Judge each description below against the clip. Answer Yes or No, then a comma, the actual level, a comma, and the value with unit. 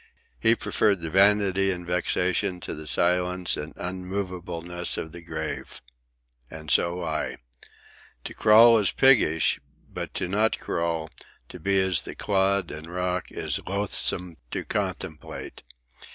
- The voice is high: No, very low, 90 Hz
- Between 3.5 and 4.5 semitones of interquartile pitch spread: No, average, 2.8 semitones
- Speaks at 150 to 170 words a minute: No, slow, 135 wpm